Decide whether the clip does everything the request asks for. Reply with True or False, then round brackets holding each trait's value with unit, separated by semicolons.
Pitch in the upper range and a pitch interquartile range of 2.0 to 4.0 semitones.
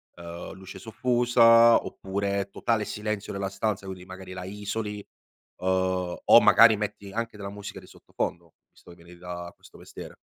False (100 Hz; 2.5 semitones)